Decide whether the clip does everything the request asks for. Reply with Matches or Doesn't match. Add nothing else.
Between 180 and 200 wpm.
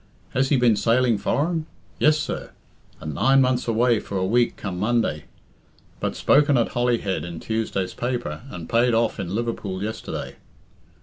Doesn't match